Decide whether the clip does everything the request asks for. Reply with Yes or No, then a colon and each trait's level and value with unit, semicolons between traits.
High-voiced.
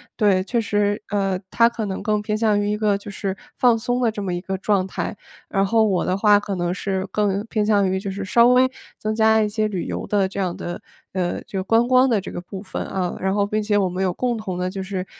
Yes: high, 205 Hz